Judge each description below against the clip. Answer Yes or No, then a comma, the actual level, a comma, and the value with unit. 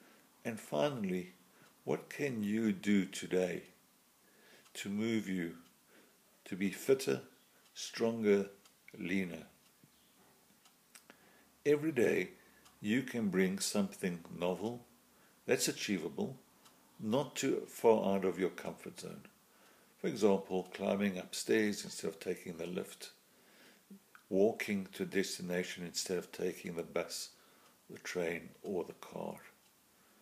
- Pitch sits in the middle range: No, low, 100 Hz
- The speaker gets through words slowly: Yes, slow, 105 wpm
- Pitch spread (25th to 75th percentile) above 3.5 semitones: Yes, average, 3.9 semitones